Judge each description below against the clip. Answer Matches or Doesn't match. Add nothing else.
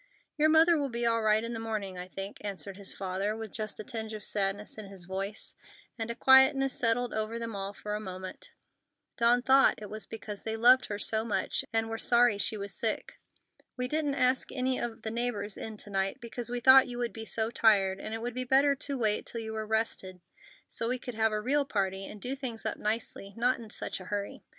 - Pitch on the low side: Doesn't match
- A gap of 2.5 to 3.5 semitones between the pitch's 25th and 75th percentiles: Matches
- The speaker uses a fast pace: Matches